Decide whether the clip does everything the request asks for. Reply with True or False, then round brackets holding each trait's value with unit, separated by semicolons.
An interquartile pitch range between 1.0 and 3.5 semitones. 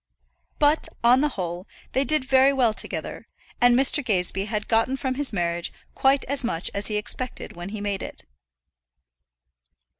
False (5.1 semitones)